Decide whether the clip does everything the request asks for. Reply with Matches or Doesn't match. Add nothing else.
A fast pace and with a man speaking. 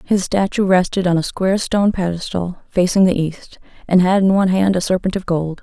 Doesn't match